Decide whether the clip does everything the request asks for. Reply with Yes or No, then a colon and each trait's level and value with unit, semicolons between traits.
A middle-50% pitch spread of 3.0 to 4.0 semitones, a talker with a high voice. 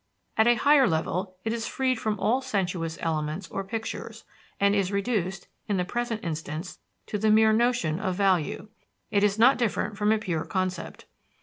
Yes: average, 3.6 semitones; high, 200 Hz